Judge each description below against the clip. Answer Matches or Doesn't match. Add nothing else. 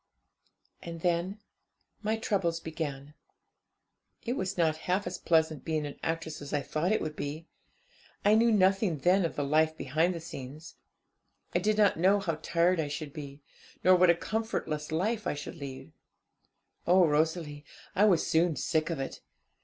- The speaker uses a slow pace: Doesn't match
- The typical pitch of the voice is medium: Matches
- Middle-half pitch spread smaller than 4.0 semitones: Matches